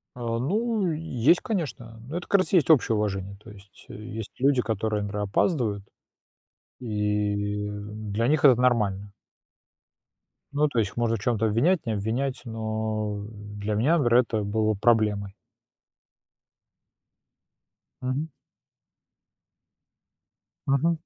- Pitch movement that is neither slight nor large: Yes, average, 4.6 semitones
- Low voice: Yes, low, 110 Hz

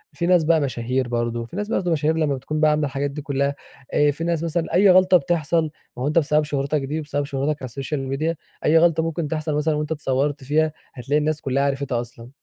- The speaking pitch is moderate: Yes, medium, 150 Hz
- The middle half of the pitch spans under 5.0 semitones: Yes, average, 2.8 semitones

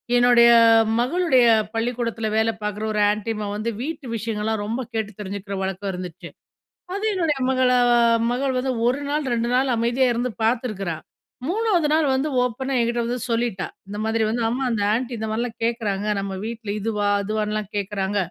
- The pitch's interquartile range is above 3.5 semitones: No, average, 3.2 semitones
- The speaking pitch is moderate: No, high, 230 Hz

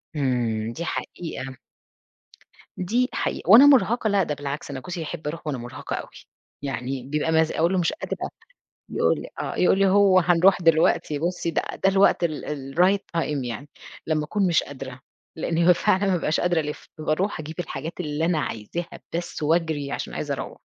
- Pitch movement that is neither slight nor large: Yes, average, 3.8 semitones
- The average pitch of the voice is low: No, medium, 160 Hz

